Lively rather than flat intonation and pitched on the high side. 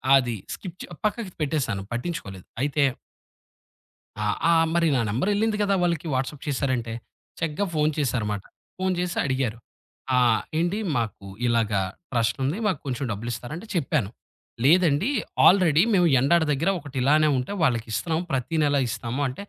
No: wide, 5.9 semitones; medium, 140 Hz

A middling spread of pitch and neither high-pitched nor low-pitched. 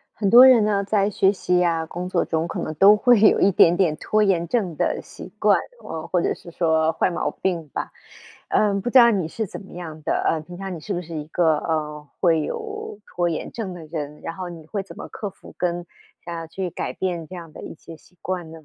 Yes: average, 3.4 semitones; medium, 175 Hz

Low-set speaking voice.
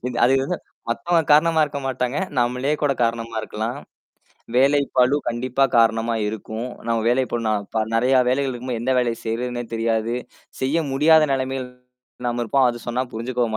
Yes: low, 125 Hz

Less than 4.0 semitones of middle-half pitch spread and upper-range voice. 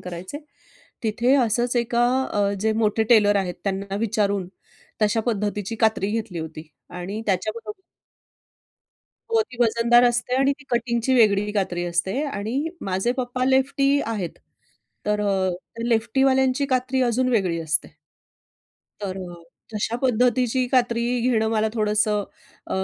Yes: average, 3.6 semitones; high, 220 Hz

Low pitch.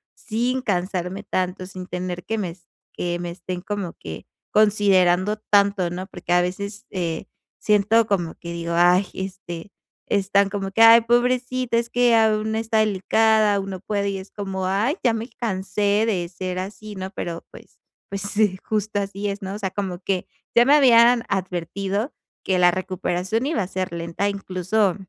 No: high, 195 Hz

